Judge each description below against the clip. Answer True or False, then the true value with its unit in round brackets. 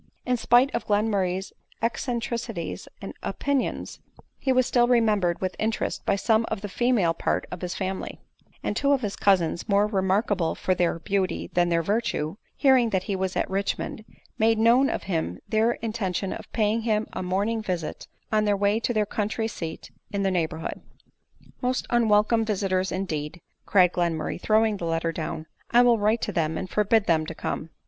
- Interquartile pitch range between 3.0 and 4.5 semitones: True (3.8 semitones)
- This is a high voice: True (205 Hz)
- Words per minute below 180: False (190 wpm)